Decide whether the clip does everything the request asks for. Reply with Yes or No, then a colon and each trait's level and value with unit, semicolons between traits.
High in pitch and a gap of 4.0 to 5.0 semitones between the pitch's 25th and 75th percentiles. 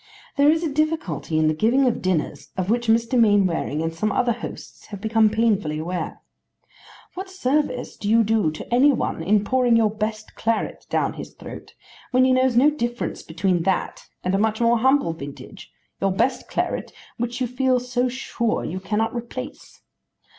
Yes: high, 225 Hz; average, 4.6 semitones